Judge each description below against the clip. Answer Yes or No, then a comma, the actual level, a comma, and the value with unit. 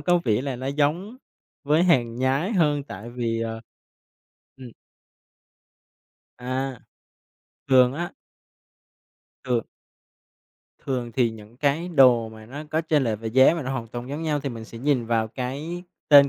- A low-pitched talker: Yes, low, 130 Hz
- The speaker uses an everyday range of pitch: Yes, average, 3.9 semitones